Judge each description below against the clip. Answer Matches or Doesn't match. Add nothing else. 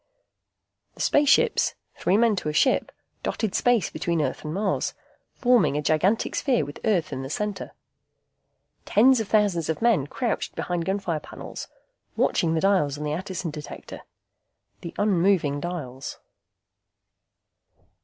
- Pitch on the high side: Doesn't match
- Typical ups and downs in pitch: Doesn't match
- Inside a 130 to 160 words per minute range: Matches